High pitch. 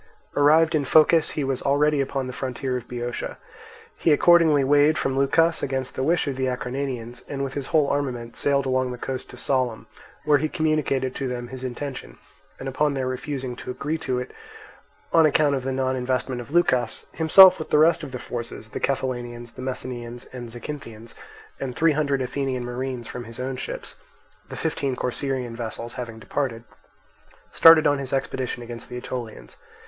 No: low, 130 Hz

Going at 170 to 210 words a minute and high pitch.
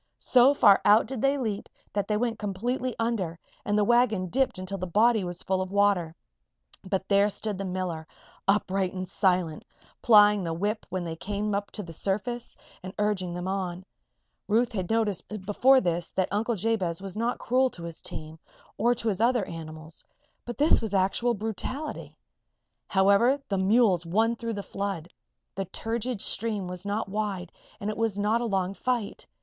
Yes: average, 175 wpm; high, 205 Hz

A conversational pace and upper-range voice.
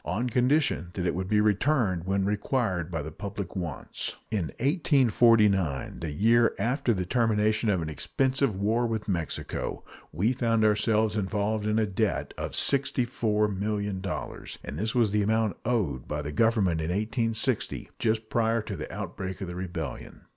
No: average, 160 wpm; low, 105 Hz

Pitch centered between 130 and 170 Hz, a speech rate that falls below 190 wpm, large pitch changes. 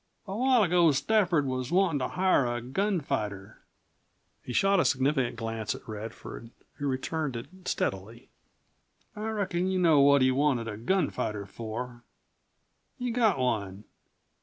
Yes: medium, 140 Hz; average, 140 wpm; wide, 8.0 semitones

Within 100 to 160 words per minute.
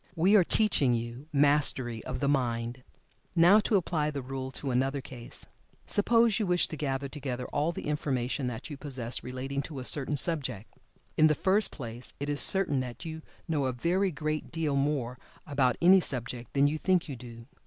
No: average, 190 wpm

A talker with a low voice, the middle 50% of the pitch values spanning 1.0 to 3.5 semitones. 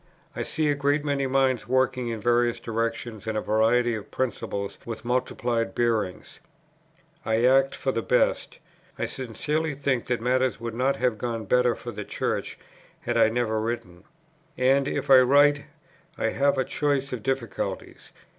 Yes: low, 125 Hz; average, 2.7 semitones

